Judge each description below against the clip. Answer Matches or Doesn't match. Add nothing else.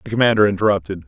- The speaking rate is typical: Matches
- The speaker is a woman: Doesn't match